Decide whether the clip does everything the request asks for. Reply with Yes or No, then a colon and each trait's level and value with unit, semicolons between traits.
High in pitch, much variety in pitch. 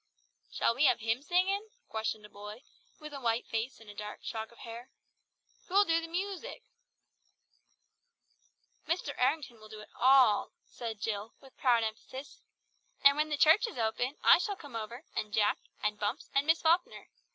Yes: very high, 250 Hz; wide, 5.9 semitones